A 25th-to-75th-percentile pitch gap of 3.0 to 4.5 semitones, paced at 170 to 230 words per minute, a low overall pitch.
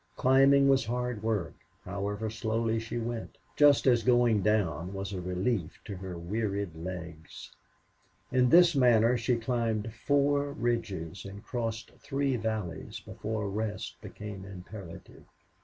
No: average, 3.8 semitones; slow, 135 wpm; low, 110 Hz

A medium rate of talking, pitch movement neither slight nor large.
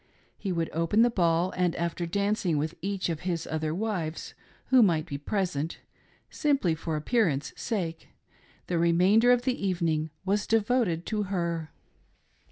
Yes: average, 160 wpm; average, 4.0 semitones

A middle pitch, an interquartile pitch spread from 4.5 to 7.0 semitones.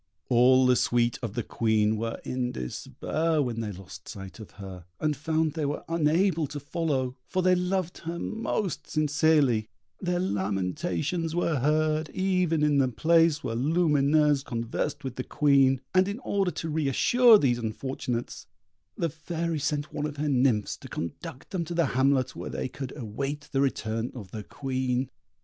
Yes: medium, 145 Hz; average, 4.9 semitones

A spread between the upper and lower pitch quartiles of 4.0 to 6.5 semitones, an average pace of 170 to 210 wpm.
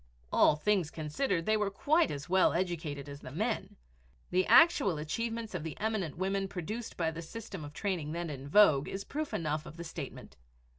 Yes: wide, 5.5 semitones; average, 190 wpm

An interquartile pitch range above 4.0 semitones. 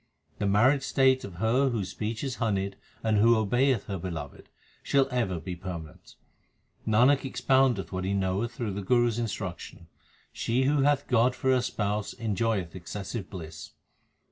Yes: average, 4.7 semitones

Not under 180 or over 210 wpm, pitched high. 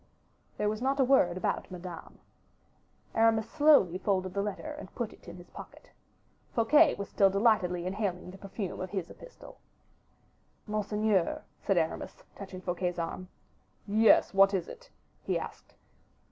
No: average, 145 wpm; high, 195 Hz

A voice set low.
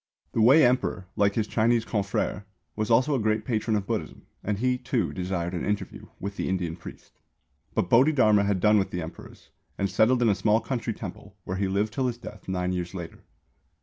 Yes: low, 105 Hz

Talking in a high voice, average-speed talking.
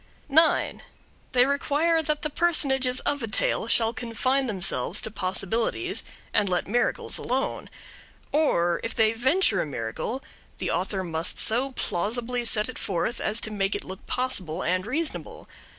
Yes: high, 230 Hz; average, 150 wpm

